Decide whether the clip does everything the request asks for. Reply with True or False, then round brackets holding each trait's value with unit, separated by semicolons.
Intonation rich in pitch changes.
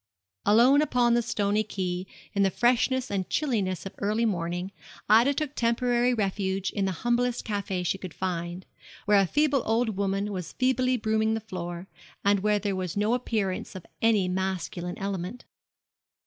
False (4.0 semitones)